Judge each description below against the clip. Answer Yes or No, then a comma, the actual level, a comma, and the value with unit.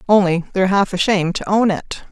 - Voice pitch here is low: No, high, 190 Hz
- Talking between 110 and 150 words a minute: No, average, 200 wpm